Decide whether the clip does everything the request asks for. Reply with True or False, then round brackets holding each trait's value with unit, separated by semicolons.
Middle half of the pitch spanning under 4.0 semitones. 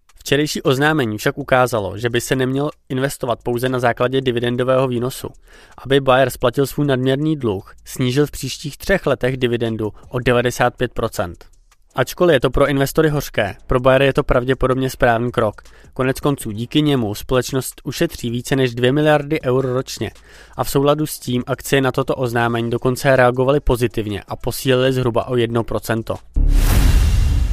True (2.5 semitones)